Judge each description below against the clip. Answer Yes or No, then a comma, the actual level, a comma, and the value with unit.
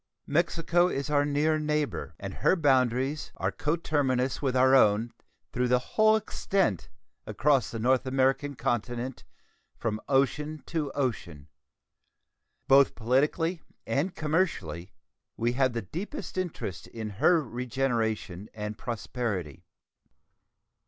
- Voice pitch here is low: Yes, low, 130 Hz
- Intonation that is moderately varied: Yes, average, 4.4 semitones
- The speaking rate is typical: No, slow, 115 wpm